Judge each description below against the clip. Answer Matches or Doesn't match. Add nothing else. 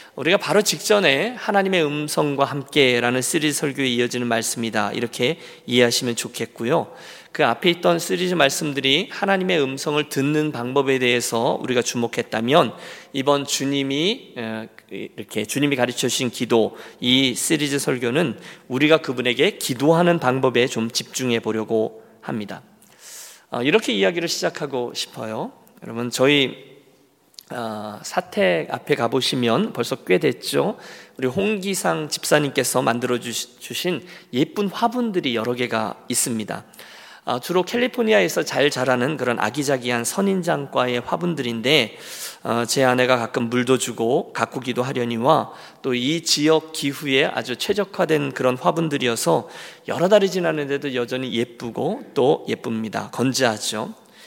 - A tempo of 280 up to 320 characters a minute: Matches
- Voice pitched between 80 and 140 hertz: Matches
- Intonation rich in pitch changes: Doesn't match